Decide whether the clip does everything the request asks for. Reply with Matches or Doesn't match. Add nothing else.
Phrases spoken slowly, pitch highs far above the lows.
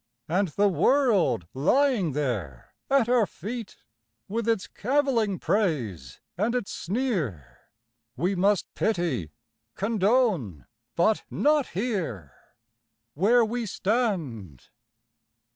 Matches